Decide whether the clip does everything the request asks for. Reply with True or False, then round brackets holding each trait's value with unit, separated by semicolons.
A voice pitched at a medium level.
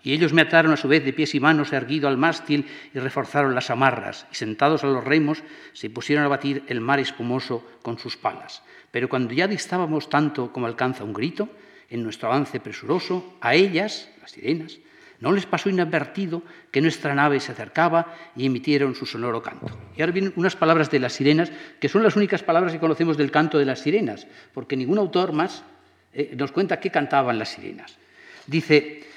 True (150 Hz)